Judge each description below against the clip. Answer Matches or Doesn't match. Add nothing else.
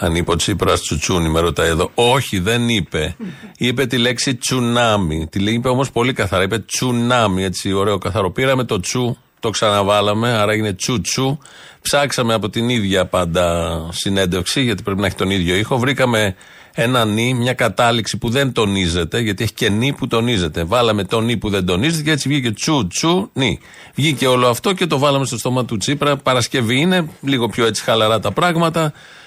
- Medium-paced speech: Doesn't match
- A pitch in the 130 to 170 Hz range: Doesn't match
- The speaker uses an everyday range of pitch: Matches